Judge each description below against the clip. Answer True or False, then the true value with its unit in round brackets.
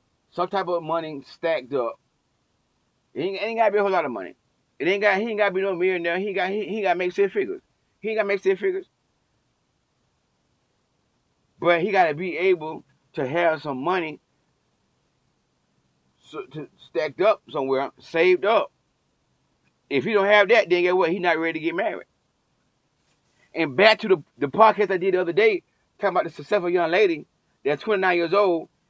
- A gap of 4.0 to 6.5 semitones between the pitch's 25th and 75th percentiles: True (4.3 semitones)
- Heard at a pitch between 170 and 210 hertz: True (190 Hz)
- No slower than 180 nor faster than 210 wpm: True (190 wpm)